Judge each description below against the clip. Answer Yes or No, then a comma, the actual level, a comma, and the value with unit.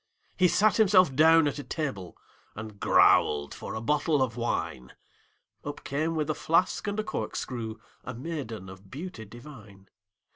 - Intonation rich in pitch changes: Yes, wide, 6.9 semitones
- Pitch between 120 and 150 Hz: Yes, medium, 140 Hz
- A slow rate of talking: No, average, 155 wpm